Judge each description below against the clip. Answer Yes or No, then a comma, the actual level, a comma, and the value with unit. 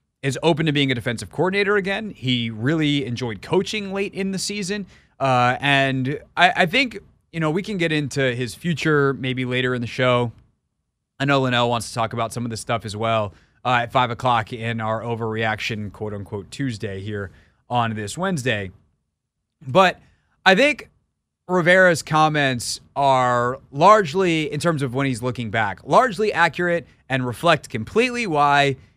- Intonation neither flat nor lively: No, wide, 6.4 semitones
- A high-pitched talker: No, low, 135 Hz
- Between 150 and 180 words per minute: Yes, average, 170 wpm